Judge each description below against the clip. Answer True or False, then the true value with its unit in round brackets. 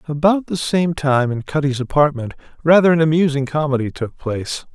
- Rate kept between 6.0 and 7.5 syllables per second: False (5.4 syllables/s)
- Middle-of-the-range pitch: True (150 Hz)